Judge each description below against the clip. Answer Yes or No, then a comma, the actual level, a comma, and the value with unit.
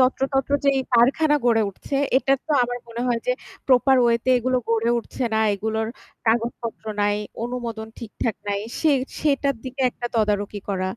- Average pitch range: Yes, average, 3.0 semitones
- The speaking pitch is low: No, high, 235 Hz